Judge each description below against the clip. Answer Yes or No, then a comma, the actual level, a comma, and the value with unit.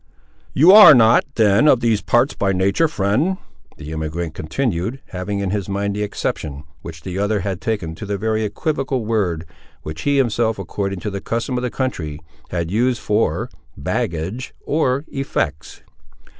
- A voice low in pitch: Yes, low, 105 Hz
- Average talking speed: Yes, average, 165 wpm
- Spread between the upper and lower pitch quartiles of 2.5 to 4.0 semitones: No, wide, 5.5 semitones